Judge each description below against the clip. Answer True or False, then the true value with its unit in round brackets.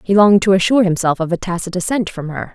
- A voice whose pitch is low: False (185 Hz)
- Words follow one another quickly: True (260 wpm)